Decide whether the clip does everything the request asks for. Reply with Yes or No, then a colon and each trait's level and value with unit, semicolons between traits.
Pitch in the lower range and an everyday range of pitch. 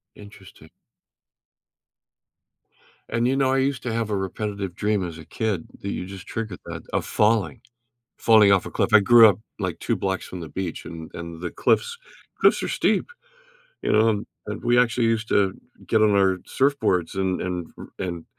Yes: low, 100 Hz; average, 3.6 semitones